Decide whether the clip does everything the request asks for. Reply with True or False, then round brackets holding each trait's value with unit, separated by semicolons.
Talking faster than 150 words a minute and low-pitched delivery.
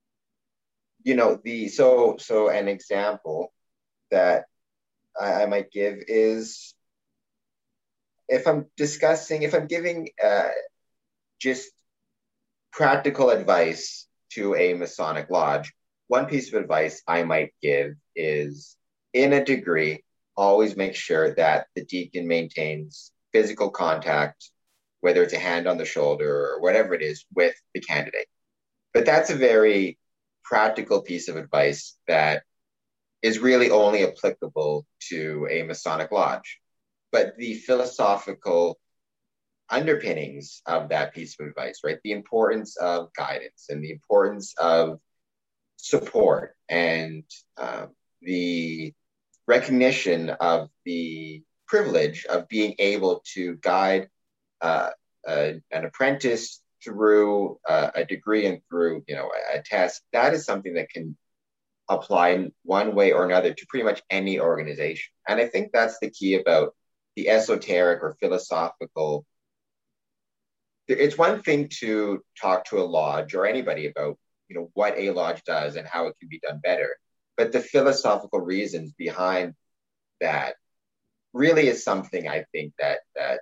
False (135 wpm; 105 Hz)